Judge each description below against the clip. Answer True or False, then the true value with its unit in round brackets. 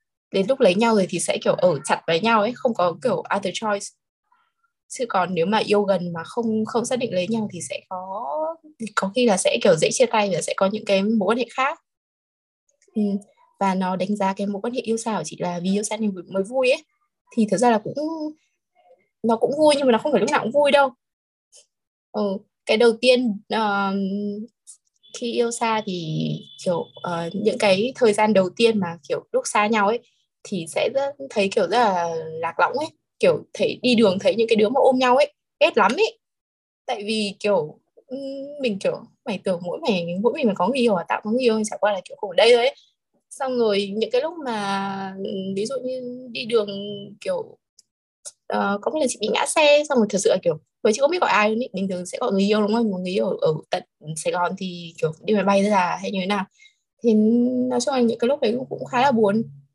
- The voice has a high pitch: True (220 Hz)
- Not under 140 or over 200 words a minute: False (235 wpm)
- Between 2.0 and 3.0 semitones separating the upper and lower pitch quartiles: False (5.0 semitones)